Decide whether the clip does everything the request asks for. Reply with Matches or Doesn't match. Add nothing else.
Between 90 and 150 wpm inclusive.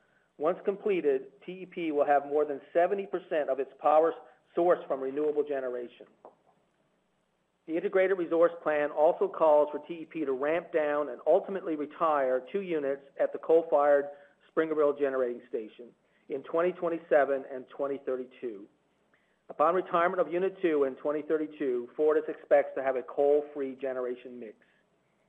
Matches